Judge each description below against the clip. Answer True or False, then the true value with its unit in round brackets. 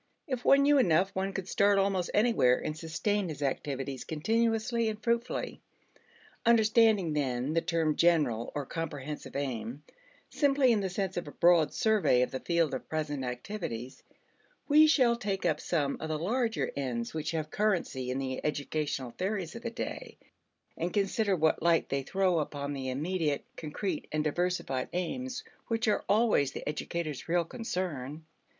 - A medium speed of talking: True (160 wpm)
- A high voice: False (170 Hz)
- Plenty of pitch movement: True (6.5 semitones)